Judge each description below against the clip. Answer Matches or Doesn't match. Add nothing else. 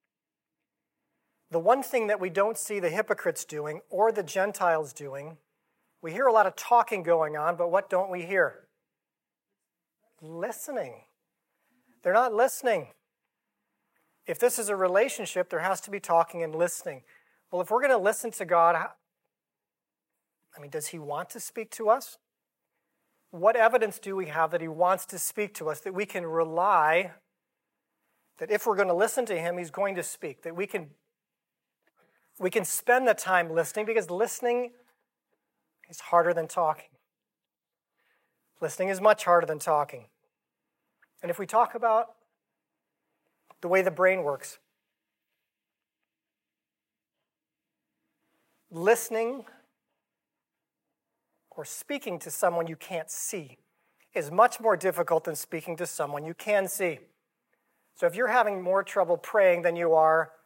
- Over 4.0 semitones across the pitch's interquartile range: Matches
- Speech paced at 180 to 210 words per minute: Doesn't match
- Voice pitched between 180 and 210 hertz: Matches